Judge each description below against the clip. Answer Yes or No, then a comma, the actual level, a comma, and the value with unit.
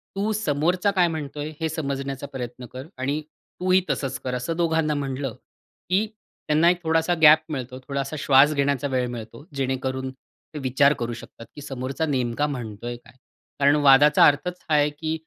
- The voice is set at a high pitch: No, medium, 145 Hz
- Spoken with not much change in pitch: No, average, 3.2 semitones